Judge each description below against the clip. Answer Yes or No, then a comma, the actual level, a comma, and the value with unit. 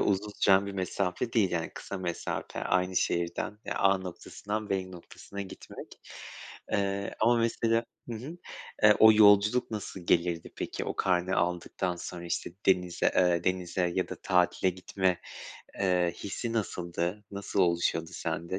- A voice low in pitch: Yes, very low, 95 Hz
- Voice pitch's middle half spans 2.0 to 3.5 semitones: Yes, narrow, 2.5 semitones